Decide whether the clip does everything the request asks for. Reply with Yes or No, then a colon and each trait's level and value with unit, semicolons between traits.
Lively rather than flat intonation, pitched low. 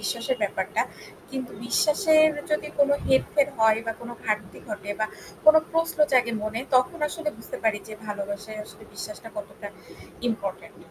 No: wide, 6.0 semitones; high, 230 Hz